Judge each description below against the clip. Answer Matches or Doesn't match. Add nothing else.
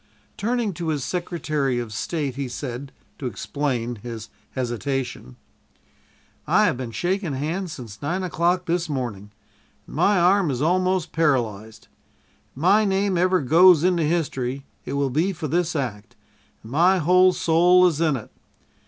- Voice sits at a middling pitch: Matches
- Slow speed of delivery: Doesn't match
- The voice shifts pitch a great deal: Matches